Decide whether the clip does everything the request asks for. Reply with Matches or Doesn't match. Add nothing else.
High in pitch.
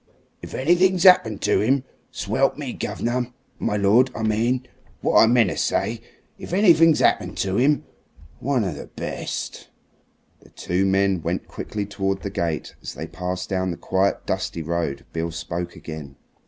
Doesn't match